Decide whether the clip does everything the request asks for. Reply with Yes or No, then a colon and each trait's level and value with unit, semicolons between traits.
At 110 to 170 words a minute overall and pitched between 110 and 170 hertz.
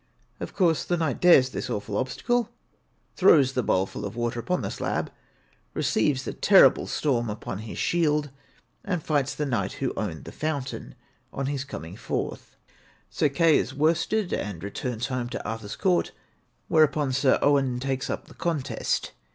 Yes: average, 165 wpm; low, 135 Hz